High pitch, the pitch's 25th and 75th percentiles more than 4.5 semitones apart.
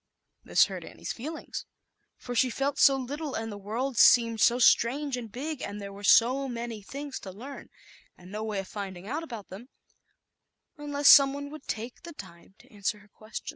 Yes: high, 235 Hz; average, 4.9 semitones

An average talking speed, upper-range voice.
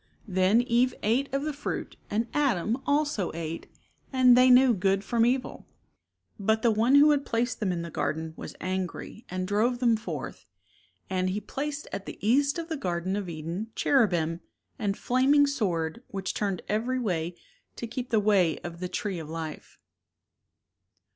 Yes: average, 175 wpm; high, 215 Hz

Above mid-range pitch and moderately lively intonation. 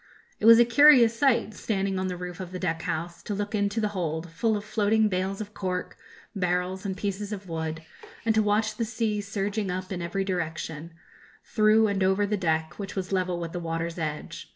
Yes: high, 195 Hz; average, 3.2 semitones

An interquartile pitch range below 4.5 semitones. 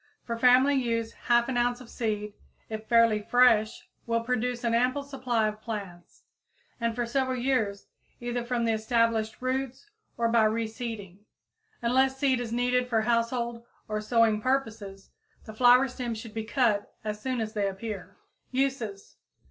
Yes: narrow, 2.4 semitones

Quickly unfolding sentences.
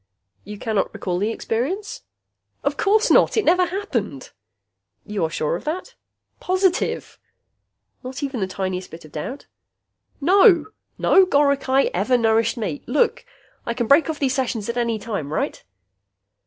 No: average, 150 wpm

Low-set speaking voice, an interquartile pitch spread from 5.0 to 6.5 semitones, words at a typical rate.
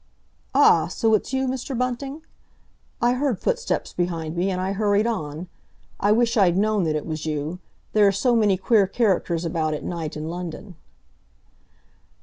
No: high, 195 Hz; wide, 5.6 semitones; average, 165 wpm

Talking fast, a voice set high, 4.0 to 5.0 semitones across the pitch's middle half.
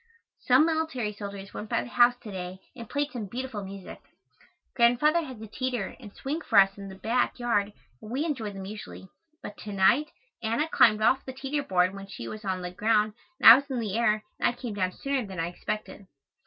Yes: fast, 220 wpm; high, 220 Hz; average, 4.5 semitones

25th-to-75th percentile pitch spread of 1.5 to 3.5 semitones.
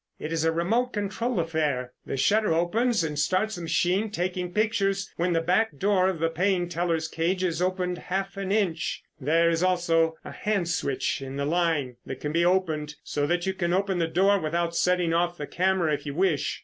Yes: average, 2.8 semitones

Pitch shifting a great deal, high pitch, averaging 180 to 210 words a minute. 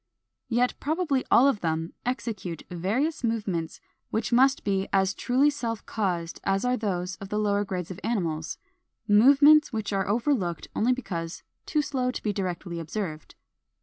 No: wide, 5.7 semitones; high, 210 Hz; average, 155 wpm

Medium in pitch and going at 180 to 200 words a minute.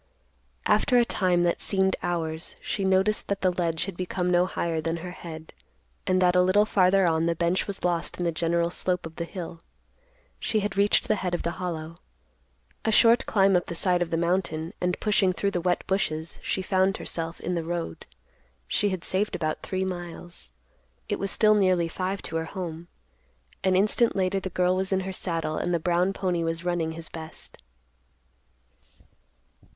Yes: medium, 180 Hz; average, 190 wpm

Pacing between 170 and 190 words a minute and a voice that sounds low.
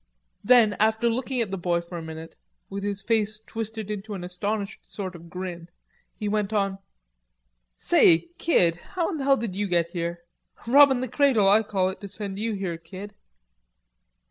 No: average, 175 wpm; high, 200 Hz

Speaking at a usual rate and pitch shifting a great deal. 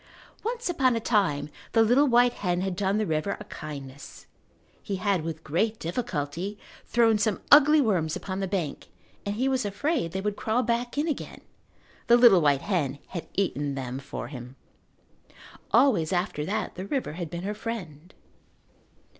Yes: average, 170 wpm; wide, 6.6 semitones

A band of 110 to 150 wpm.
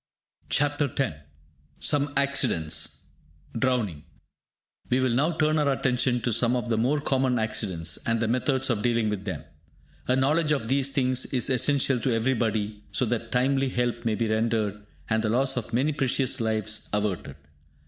No: average, 165 wpm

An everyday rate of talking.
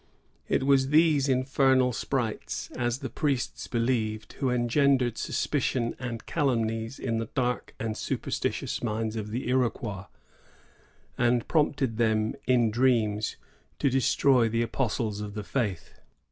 No: slow, 130 wpm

